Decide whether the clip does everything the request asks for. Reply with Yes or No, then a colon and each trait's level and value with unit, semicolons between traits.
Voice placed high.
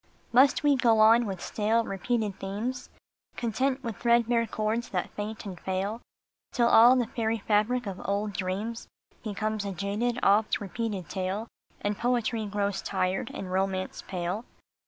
Yes: high, 215 Hz